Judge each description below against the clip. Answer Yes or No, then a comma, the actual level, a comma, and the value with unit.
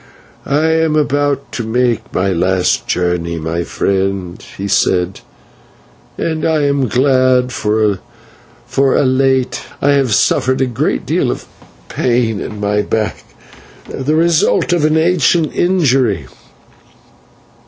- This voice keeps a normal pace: No, slow, 120 wpm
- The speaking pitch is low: Yes, low, 130 Hz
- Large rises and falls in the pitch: Yes, wide, 5.9 semitones